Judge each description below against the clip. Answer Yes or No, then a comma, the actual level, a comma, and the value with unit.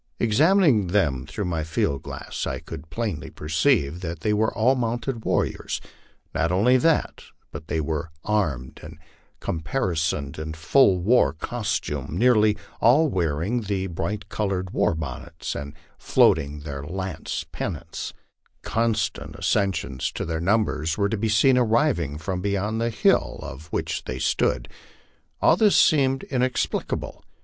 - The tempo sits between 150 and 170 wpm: No, average, 140 wpm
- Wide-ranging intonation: Yes, wide, 6.3 semitones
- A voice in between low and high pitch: No, very low, 95 Hz